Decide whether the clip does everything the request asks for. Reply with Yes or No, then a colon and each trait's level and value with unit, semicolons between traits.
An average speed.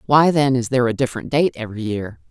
No: fast, 235 wpm